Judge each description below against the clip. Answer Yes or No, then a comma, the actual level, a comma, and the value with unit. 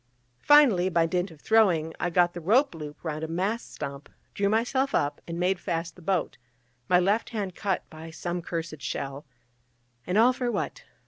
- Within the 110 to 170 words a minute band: No, average, 185 wpm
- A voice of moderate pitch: Yes, medium, 175 Hz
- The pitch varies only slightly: No, average, 4.3 semitones